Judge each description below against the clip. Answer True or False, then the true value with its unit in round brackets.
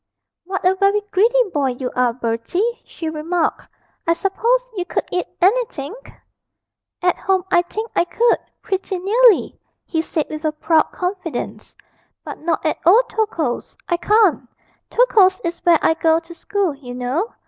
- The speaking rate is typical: True (160 wpm)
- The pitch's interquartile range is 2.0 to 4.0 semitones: False (4.4 semitones)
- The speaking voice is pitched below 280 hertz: False (355 Hz)